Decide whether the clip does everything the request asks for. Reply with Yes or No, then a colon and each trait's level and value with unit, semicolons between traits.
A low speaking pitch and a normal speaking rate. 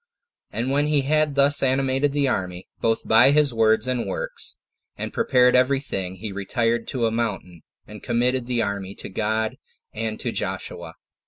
Yes: low, 120 Hz; average, 170 wpm